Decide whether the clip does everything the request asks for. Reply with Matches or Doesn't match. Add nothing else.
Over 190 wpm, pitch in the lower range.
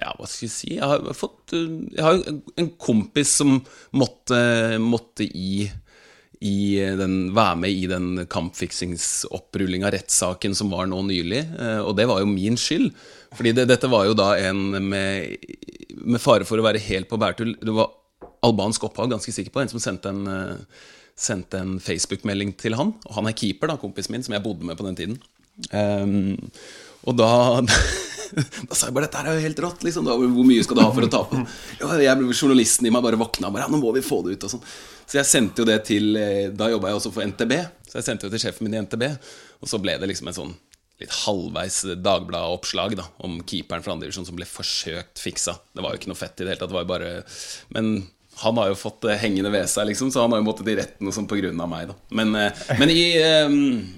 Matches